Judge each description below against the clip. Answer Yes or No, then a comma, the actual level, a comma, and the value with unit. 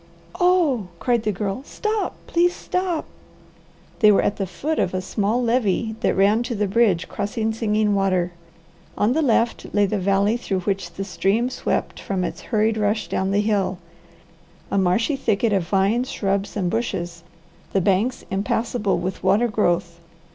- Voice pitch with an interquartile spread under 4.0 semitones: Yes, average, 3.4 semitones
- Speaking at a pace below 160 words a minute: No, average, 165 wpm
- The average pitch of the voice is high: Yes, high, 210 Hz